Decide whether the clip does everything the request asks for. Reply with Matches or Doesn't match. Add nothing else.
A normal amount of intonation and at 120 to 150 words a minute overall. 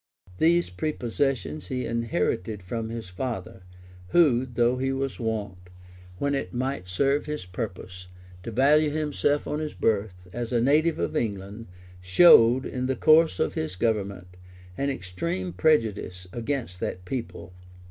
Doesn't match